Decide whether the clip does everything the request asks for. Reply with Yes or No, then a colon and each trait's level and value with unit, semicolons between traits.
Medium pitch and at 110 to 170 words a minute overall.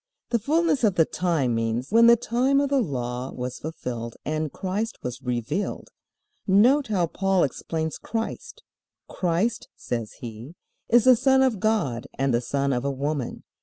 Yes: medium, 165 Hz; average, 165 wpm